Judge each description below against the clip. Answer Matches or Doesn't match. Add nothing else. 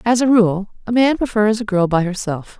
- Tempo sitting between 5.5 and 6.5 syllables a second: Doesn't match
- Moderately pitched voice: Doesn't match